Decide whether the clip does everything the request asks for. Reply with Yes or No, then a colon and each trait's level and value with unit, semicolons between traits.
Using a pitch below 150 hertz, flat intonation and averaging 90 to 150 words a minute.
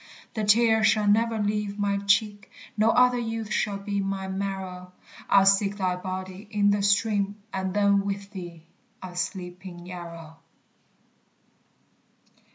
No: high, 200 Hz; narrow, 1.9 semitones; average, 140 wpm